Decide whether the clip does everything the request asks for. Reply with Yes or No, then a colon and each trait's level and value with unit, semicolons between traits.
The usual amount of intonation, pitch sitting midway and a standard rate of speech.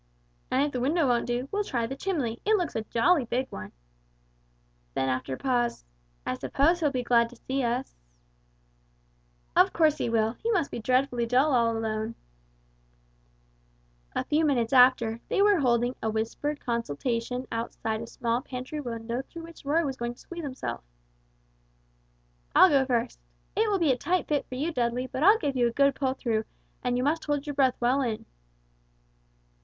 No: average, 3.8 semitones; very high, 255 Hz; average, 180 wpm